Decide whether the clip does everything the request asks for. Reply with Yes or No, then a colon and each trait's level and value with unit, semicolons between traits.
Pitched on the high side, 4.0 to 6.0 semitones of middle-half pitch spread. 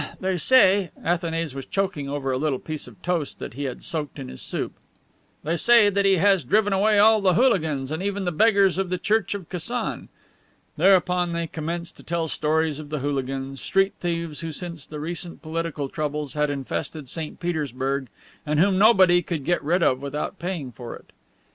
No: medium, 165 Hz; average, 4.4 semitones